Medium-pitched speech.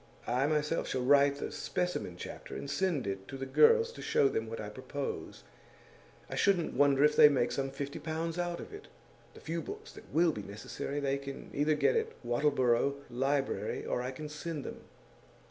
Yes: medium, 145 Hz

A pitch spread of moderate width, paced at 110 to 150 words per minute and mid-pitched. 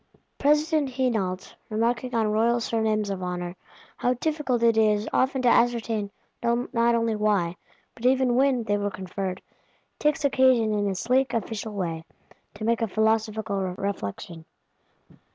No: average, 3.3 semitones; average, 140 wpm; high, 225 Hz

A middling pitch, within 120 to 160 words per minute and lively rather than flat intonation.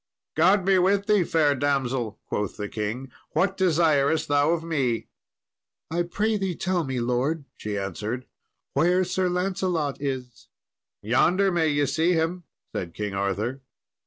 Yes: medium, 150 Hz; average, 145 wpm; wide, 6.3 semitones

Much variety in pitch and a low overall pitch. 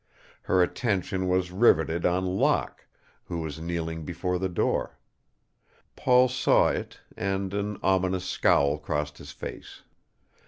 No: average, 2.7 semitones; very low, 90 Hz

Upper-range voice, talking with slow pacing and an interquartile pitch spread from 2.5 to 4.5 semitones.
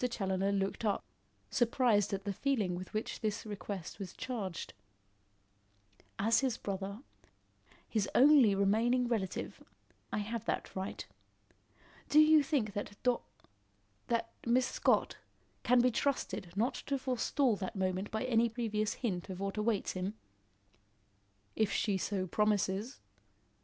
Yes: high, 215 Hz; slow, 130 wpm; average, 3.6 semitones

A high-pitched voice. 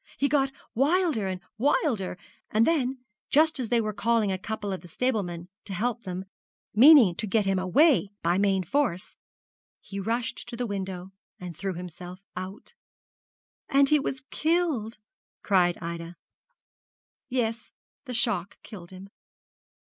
Yes: high, 215 Hz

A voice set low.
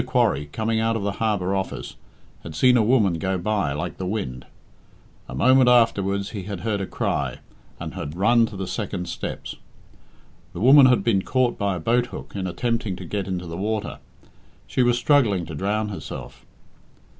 Yes: low, 100 Hz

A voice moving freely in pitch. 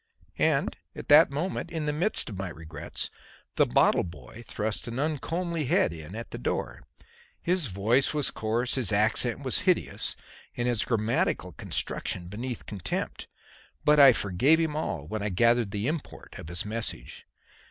Yes: wide, 6.7 semitones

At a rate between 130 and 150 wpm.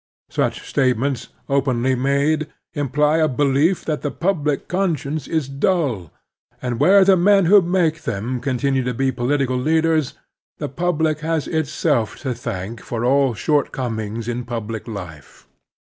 Yes: average, 140 wpm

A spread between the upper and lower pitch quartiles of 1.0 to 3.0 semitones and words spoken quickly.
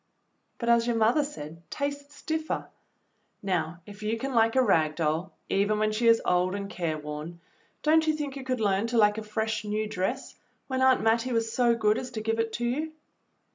No: average, 4.3 semitones; fast, 210 wpm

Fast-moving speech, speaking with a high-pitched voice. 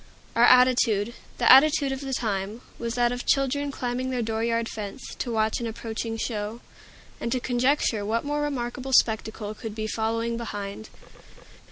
No: average, 160 wpm; high, 235 Hz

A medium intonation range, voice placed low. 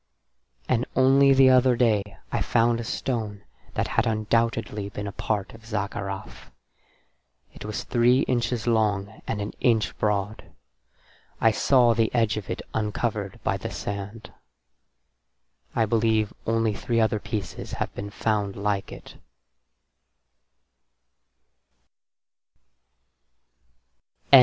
No: narrow, 2.3 semitones; low, 110 Hz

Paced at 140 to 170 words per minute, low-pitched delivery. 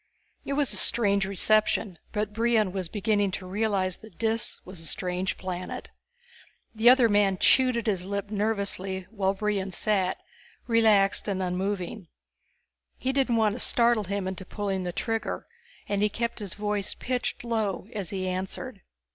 No: average, 160 wpm; high, 205 Hz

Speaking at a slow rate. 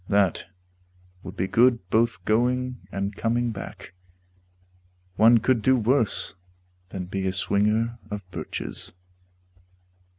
Yes: slow, 110 wpm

